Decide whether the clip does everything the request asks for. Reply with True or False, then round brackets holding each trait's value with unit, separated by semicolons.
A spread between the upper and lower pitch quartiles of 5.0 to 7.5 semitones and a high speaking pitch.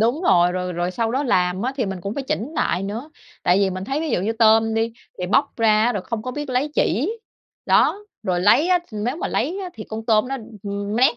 True (5.4 semitones; 225 Hz)